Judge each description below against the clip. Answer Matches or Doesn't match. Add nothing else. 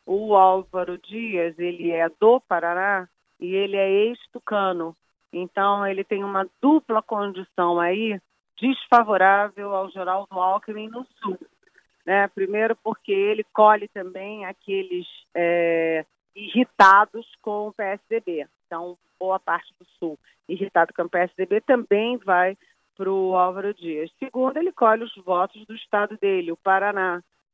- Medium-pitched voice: Doesn't match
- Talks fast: Doesn't match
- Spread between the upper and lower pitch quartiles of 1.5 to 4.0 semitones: Matches